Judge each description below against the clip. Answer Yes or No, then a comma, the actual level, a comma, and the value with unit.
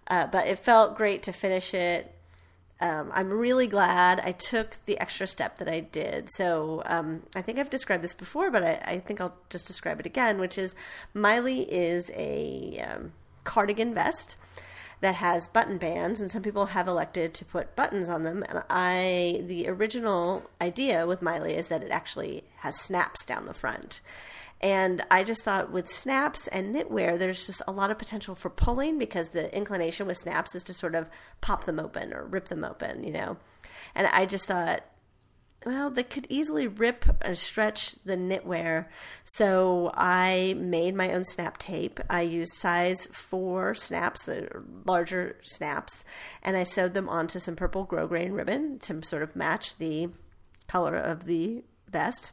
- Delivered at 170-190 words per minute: Yes, average, 175 wpm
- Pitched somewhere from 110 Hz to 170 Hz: No, medium, 185 Hz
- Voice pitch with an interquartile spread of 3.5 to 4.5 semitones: No, average, 3.0 semitones